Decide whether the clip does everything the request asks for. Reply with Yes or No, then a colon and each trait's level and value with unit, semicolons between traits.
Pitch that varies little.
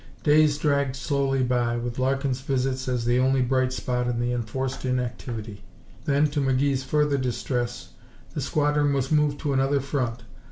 Yes: narrow, 2.3 semitones